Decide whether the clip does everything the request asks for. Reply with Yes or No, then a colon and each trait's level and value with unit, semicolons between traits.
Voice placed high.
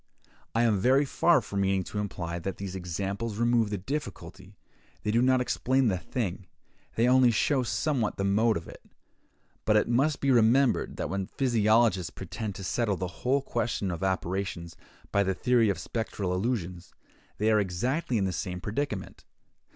No: low, 105 Hz